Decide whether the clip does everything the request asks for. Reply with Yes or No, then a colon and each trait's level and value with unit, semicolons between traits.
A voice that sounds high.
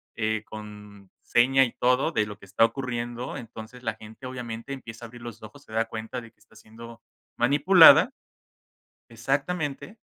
No: low, 115 Hz